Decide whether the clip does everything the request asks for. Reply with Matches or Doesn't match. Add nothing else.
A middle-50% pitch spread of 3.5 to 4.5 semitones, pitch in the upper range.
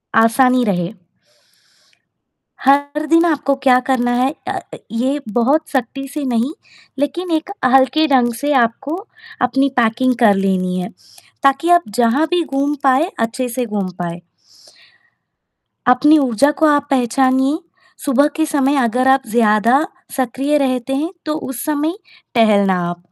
Matches